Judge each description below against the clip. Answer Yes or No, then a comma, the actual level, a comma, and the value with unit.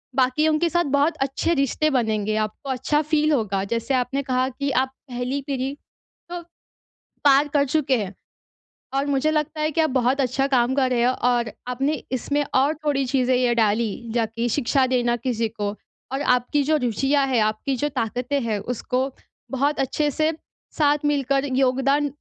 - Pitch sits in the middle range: No, very high, 265 Hz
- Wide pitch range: No, average, 2.9 semitones